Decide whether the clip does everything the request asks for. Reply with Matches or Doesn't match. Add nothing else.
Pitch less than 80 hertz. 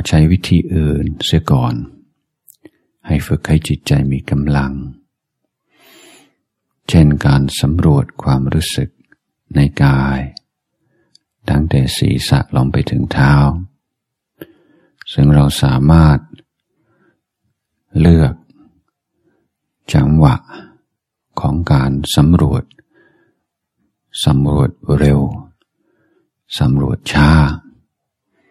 Matches